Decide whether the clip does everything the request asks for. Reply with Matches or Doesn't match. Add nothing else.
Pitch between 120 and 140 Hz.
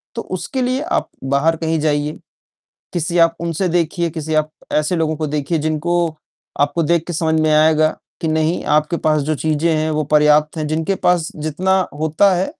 Doesn't match